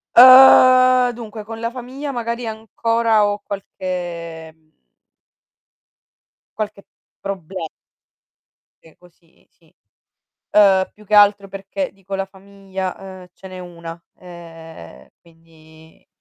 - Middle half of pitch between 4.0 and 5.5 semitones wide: Yes, average, 4.6 semitones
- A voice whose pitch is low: No, high, 195 Hz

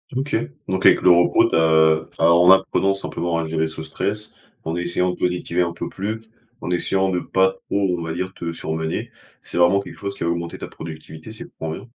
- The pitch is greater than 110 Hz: No, very low, 85 Hz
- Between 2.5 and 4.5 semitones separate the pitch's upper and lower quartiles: Yes, average, 2.8 semitones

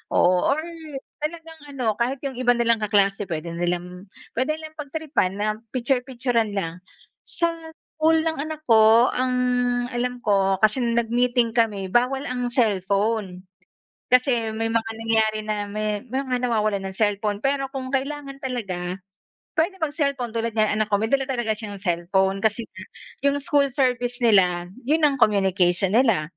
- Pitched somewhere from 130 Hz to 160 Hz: No, high, 230 Hz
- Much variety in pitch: No, average, 4.7 semitones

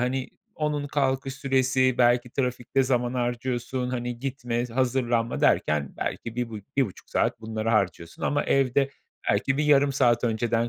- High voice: No, low, 125 Hz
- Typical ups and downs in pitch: No, narrow, 2.2 semitones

